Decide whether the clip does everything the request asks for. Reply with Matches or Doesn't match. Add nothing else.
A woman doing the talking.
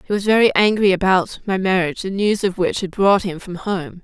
Matches